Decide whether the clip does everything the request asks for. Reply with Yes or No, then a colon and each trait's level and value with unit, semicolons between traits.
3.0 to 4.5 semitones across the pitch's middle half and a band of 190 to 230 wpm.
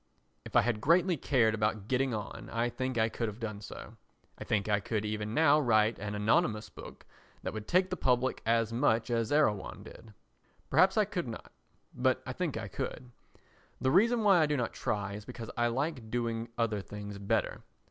Yes: average, 3.9 semitones; average, 200 wpm